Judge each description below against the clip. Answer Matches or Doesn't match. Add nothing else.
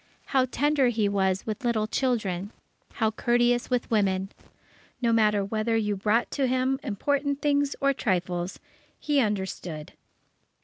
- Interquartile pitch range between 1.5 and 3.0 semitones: Doesn't match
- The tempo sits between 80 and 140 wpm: Matches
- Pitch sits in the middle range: Doesn't match